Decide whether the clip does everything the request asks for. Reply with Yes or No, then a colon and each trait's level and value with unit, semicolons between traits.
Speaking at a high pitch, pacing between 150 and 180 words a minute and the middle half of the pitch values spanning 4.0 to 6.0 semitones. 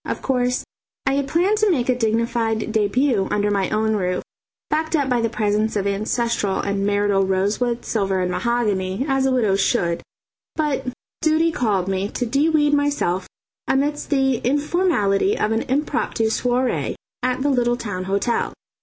Yes: high, 235 Hz; average, 165 wpm; average, 5.0 semitones